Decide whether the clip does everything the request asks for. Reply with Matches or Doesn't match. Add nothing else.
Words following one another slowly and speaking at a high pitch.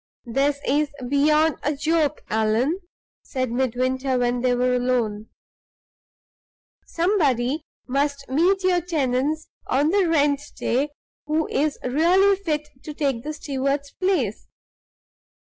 Matches